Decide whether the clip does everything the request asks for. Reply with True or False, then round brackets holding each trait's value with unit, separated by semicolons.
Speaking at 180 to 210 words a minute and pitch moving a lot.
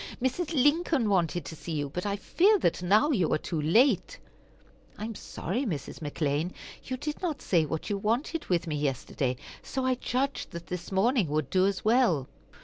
True (190 wpm; 8.1 semitones)